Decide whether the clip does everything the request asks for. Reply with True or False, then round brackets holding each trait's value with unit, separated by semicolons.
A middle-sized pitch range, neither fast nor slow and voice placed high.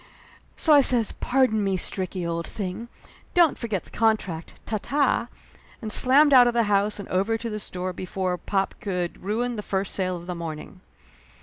True (4.4 semitones; 185 wpm; 205 Hz)